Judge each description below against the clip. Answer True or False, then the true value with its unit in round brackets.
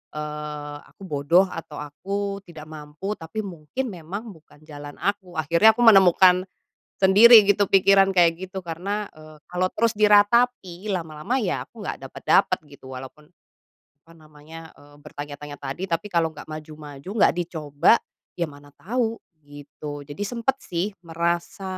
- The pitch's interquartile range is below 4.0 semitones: False (4.8 semitones)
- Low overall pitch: False (170 Hz)